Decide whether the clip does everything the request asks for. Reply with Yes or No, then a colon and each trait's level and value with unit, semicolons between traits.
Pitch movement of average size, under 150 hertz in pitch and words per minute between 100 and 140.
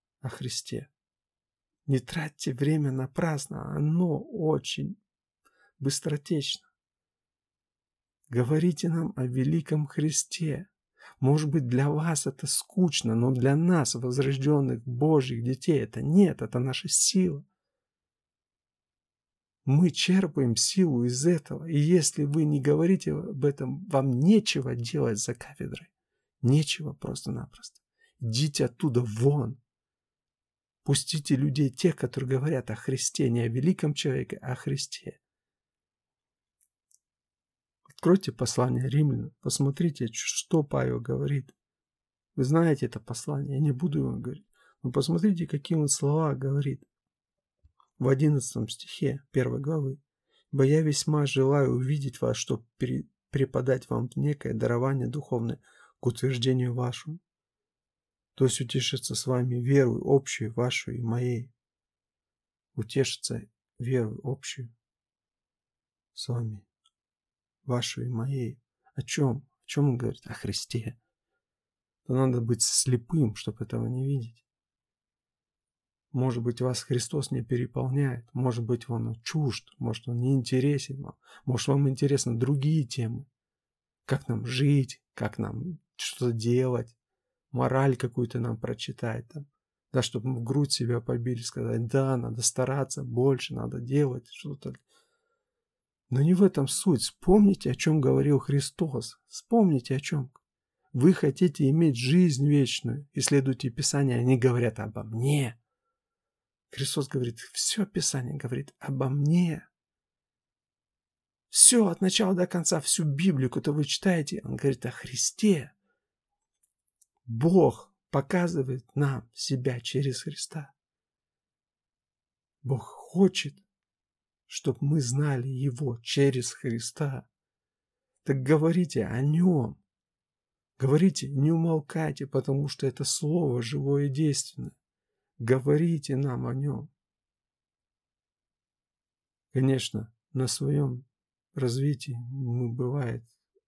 Yes: average, 3.6 semitones; low, 135 Hz; average, 115 wpm